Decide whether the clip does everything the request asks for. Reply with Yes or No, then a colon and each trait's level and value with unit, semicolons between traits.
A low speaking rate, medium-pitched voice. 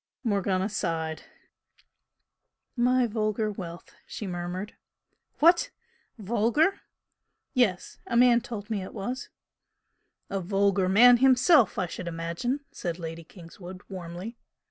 No: slow, 110 wpm; high, 200 Hz